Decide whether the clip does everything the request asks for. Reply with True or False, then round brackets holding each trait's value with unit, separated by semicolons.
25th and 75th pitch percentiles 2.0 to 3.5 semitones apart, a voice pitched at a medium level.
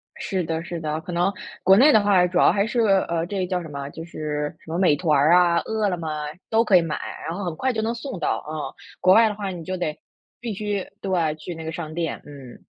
False (3.9 semitones; 175 Hz)